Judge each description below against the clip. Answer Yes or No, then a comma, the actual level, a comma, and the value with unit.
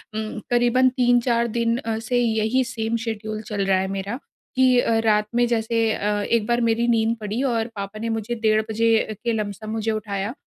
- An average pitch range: No, narrow, 1.7 semitones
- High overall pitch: Yes, high, 225 Hz